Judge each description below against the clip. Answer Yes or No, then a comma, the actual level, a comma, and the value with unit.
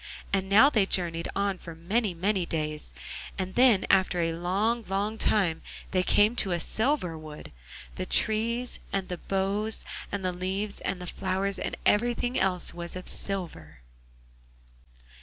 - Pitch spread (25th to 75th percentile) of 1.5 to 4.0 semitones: Yes, average, 3.2 semitones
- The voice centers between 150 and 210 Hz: Yes, high, 190 Hz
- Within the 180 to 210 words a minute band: No, average, 155 wpm